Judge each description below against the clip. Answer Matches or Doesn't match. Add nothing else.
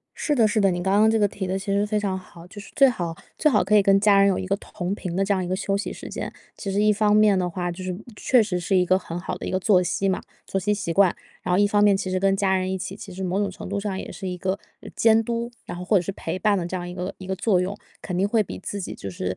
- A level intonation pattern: Matches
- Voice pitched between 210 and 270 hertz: Doesn't match